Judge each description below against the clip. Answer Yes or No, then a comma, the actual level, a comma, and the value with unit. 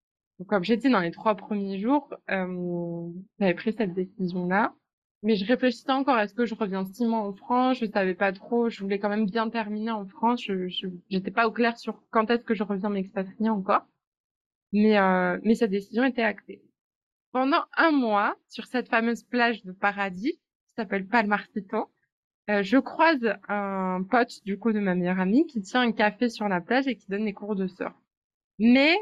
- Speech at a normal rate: Yes, average, 200 wpm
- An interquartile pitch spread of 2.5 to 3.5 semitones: Yes, average, 3.2 semitones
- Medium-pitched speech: No, high, 215 Hz